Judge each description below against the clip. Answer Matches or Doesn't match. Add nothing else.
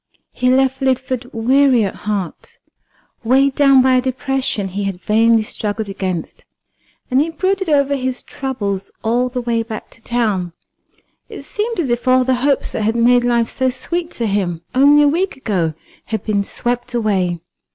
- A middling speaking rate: Matches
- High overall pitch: Matches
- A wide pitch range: Doesn't match